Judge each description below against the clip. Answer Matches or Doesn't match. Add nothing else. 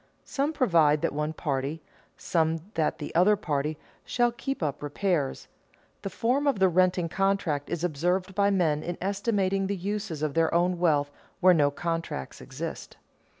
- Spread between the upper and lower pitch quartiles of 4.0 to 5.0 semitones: Matches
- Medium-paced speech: Matches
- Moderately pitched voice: Matches